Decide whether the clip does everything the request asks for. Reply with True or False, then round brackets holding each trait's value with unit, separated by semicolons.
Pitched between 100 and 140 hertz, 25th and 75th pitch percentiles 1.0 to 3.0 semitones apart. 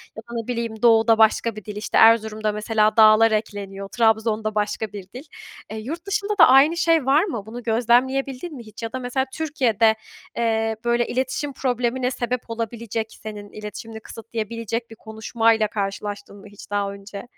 False (225 Hz; 2.4 semitones)